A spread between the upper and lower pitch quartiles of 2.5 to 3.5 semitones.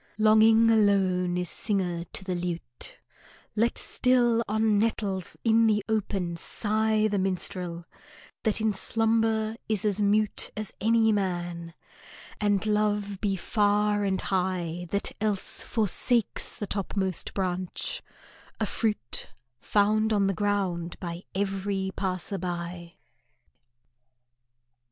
Yes: average, 2.9 semitones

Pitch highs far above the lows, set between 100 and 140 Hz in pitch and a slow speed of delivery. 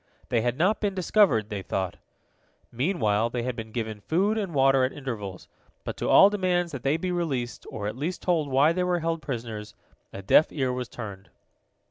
No: wide, 7.6 semitones; low, 135 Hz; average, 195 wpm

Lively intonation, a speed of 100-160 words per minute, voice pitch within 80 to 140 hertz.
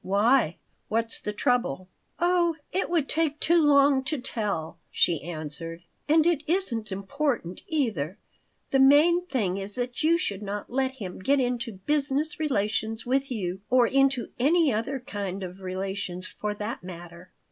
No: wide, 6.7 semitones; average, 155 wpm; high, 240 Hz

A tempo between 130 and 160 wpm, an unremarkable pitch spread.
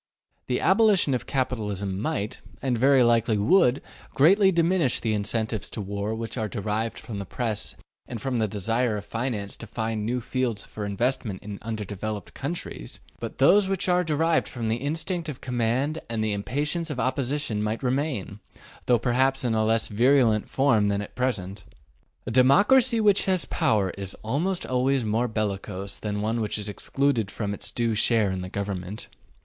No: average, 175 wpm; average, 4.5 semitones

